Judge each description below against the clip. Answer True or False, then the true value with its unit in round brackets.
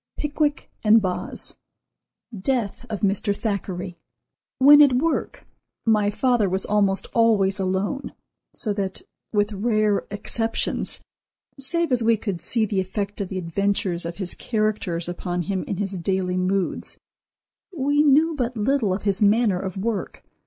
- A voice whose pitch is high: True (205 Hz)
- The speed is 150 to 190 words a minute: False (140 wpm)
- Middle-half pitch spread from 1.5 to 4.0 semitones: True (3.5 semitones)